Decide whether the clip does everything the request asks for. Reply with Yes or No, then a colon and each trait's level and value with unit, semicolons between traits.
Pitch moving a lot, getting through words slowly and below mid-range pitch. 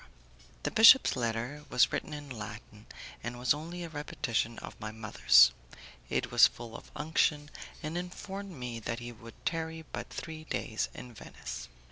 No: wide, 5.9 semitones; average, 160 wpm; low, 125 Hz